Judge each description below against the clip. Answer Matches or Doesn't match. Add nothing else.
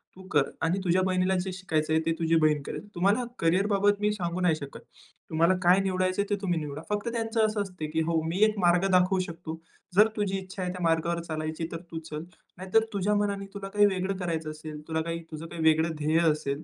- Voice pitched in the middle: Matches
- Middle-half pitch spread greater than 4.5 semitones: Doesn't match